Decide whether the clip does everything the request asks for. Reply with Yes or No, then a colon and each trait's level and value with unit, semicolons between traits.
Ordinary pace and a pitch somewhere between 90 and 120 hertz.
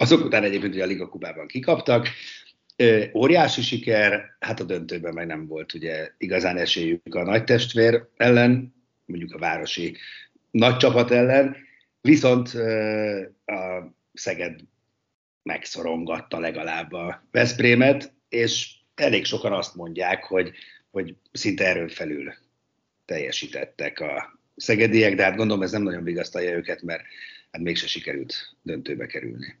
Yes: average, 130 wpm; low, 105 Hz